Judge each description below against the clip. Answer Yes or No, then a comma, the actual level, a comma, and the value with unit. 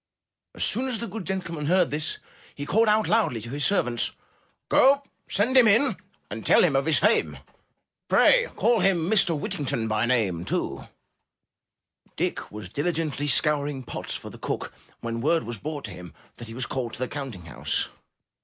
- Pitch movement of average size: No, wide, 8.6 semitones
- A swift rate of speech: No, average, 175 wpm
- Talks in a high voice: No, medium, 150 Hz